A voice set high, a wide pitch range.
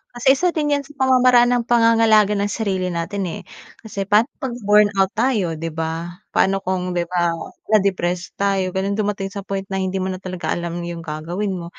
No: high, 195 Hz; average, 3.4 semitones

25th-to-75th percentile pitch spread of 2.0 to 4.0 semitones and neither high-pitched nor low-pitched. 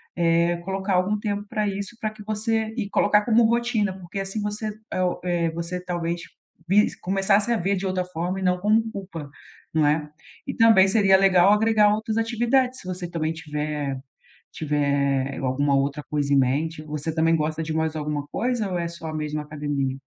No: average, 5.2 semitones; medium, 180 Hz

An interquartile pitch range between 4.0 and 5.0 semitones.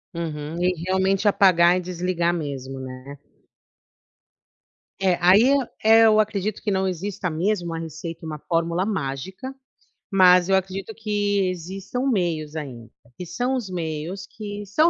No: average, 3.5 semitones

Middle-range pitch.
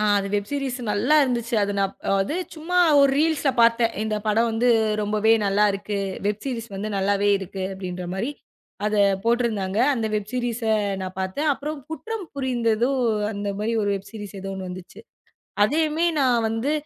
No: high, 220 Hz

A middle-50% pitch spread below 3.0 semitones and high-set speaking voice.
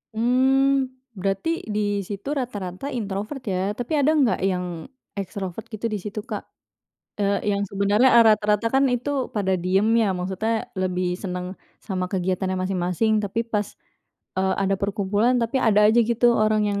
No: average, 3.3 semitones; high, 205 Hz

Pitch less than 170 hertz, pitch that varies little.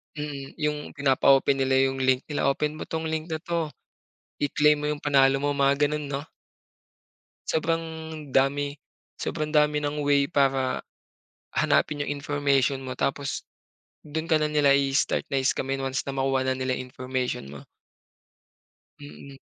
Yes: medium, 140 Hz; narrow, 1.8 semitones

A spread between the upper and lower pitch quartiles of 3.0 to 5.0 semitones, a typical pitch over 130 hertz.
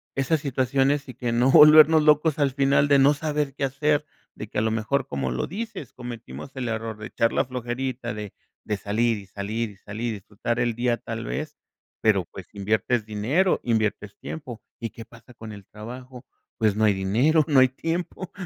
No: average, 4.4 semitones; low, 120 Hz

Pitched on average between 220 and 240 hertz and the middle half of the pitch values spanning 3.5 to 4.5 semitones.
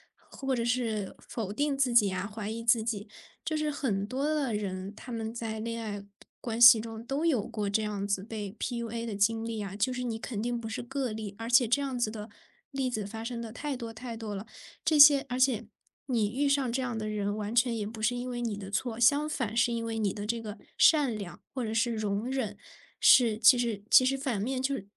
No: high, 230 Hz; average, 2.9 semitones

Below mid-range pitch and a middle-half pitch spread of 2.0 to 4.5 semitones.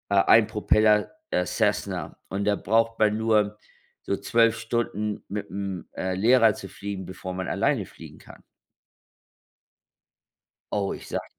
Yes: low, 105 Hz; narrow, 2.4 semitones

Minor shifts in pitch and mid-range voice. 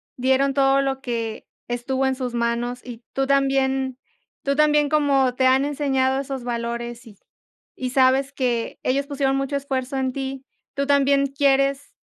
No: narrow, 1.6 semitones; very high, 270 Hz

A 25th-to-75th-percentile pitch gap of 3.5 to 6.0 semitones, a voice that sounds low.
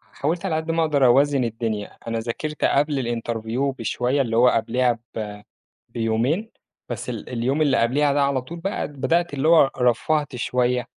Yes: average, 4.2 semitones; low, 130 Hz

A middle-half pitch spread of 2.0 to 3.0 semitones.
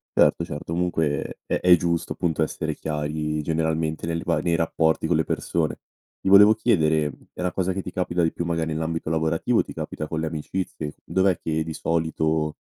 No: narrow, 1.6 semitones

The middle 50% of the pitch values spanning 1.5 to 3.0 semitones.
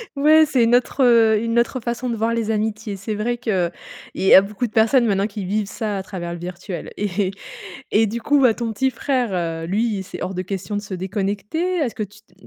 No: average, 3.5 semitones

